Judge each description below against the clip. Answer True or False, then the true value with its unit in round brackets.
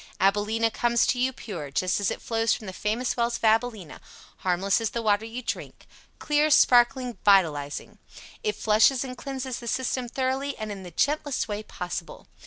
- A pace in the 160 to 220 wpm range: True (180 wpm)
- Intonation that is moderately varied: True (3.8 semitones)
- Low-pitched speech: False (225 Hz)